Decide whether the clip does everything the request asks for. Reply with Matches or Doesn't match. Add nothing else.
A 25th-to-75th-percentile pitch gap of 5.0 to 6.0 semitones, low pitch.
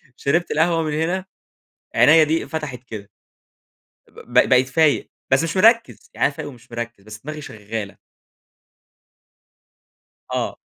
Doesn't match